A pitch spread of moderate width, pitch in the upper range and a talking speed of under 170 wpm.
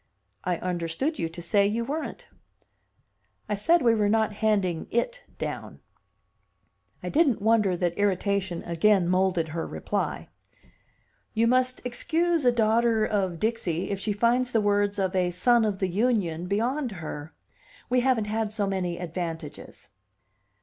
Yes: average, 4.5 semitones; high, 205 Hz; average, 145 wpm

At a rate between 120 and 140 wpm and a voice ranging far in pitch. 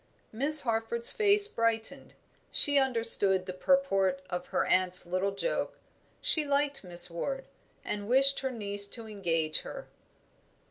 Yes: slow, 135 wpm; wide, 6.6 semitones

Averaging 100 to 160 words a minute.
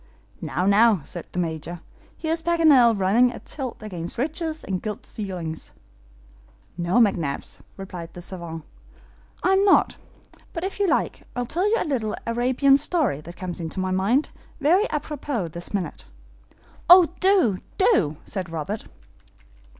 Yes: average, 145 wpm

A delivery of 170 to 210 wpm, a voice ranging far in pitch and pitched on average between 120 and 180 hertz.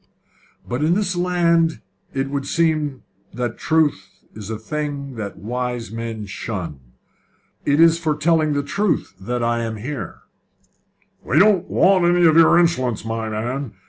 No: average, 150 wpm; wide, 6.3 semitones; medium, 140 Hz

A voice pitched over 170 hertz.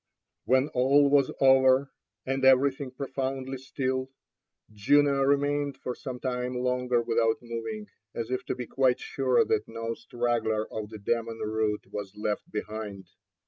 No: low, 125 Hz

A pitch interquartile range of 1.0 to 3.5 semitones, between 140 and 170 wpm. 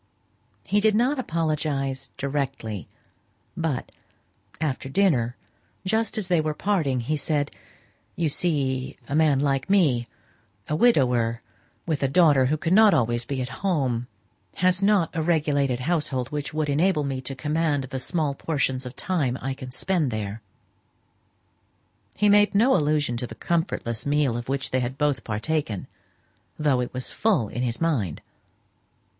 No: average, 4.3 semitones; average, 150 wpm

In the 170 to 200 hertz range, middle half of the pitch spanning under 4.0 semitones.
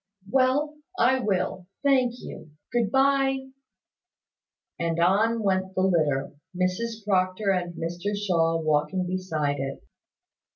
No: high, 190 Hz; average, 5.3 semitones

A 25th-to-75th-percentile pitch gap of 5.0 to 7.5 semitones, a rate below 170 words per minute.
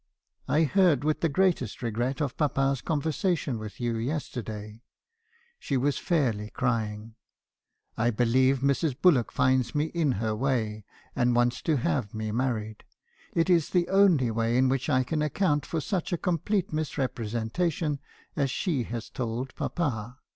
Yes: average, 5.3 semitones; average, 150 wpm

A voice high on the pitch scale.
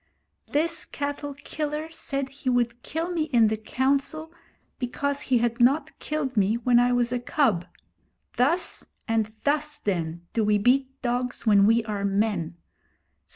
Yes: very high, 250 Hz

